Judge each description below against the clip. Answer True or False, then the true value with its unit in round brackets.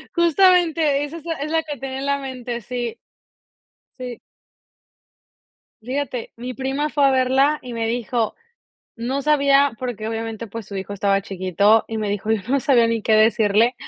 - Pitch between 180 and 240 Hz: False (250 Hz)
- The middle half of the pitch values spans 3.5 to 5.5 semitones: True (4.0 semitones)